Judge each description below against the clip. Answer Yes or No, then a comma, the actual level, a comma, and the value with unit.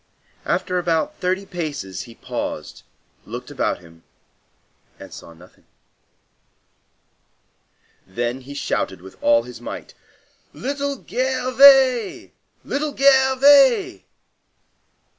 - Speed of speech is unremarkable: No, slow, 90 wpm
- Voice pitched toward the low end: No, medium, 185 Hz